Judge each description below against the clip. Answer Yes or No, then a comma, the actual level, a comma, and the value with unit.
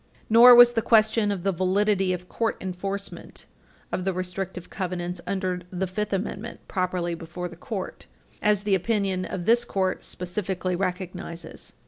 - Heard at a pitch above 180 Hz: Yes, high, 190 Hz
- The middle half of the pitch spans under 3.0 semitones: Yes, narrow, 2.5 semitones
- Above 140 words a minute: Yes, average, 150 wpm